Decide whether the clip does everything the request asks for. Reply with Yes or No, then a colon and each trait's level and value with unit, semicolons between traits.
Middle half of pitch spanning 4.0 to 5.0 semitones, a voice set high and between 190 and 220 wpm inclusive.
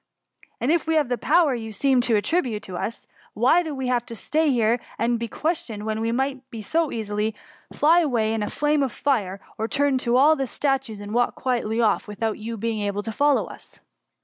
Yes: average, 4.5 semitones; high, 240 Hz; fast, 205 wpm